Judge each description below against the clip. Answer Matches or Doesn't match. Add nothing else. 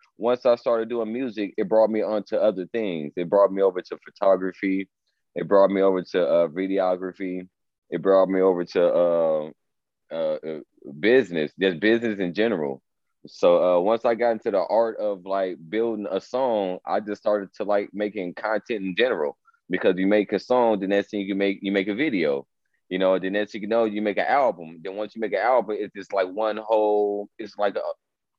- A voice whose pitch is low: Matches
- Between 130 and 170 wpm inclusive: Doesn't match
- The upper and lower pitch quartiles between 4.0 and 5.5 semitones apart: Doesn't match